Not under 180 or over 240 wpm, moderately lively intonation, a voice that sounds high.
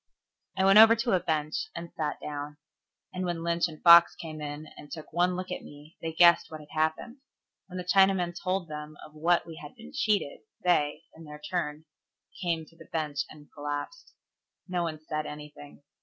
No: average, 195 wpm; average, 3.1 semitones; medium, 165 Hz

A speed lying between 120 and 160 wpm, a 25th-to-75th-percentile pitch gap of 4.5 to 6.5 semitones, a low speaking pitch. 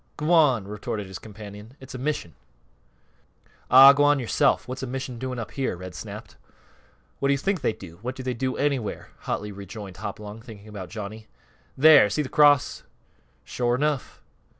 No: average, 170 wpm; average, 4.8 semitones; low, 125 Hz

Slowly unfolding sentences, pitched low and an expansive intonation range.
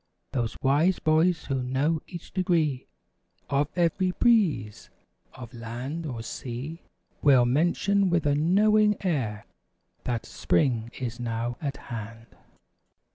No: slow, 120 wpm; medium, 145 Hz; wide, 6.1 semitones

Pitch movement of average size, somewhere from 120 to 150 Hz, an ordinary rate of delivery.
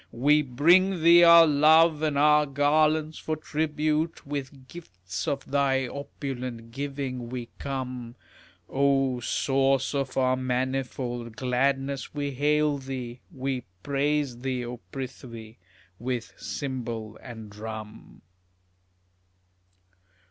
No: average, 3.0 semitones; low, 135 Hz; slow, 105 wpm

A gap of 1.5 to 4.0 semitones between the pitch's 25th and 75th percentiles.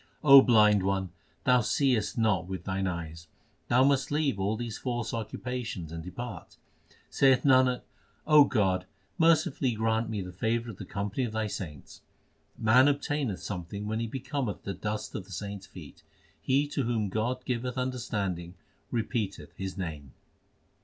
No: average, 4.8 semitones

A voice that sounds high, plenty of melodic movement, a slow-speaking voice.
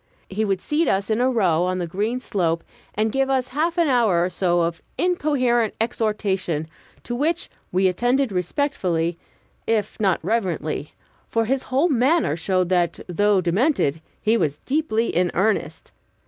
No: high, 215 Hz; wide, 6.0 semitones; average, 160 wpm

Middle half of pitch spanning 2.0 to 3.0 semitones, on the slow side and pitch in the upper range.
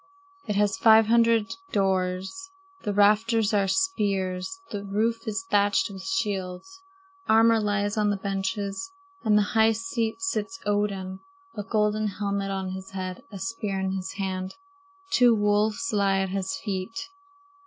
No: narrow, 2.6 semitones; average, 145 wpm; high, 205 Hz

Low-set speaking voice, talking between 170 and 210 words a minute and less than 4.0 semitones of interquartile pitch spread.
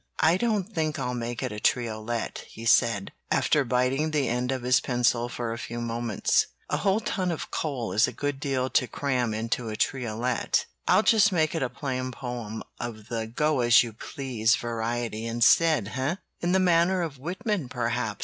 No: low, 125 Hz; average, 180 wpm; average, 4.7 semitones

